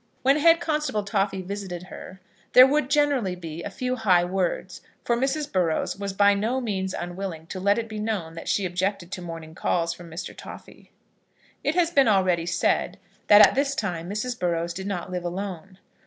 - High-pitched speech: Yes, high, 195 Hz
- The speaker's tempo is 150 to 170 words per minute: No, average, 190 wpm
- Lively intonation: No, average, 5.0 semitones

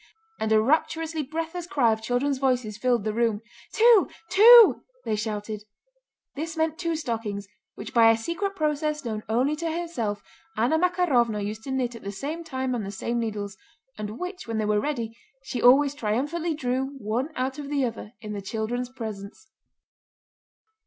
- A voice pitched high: Yes, very high, 250 Hz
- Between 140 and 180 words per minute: Yes, average, 175 wpm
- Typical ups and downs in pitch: No, wide, 6.0 semitones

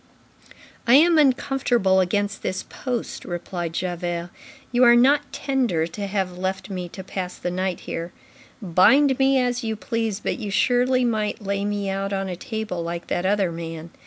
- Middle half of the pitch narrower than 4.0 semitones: No, average, 5.3 semitones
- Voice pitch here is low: No, high, 200 Hz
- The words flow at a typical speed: Yes, average, 170 wpm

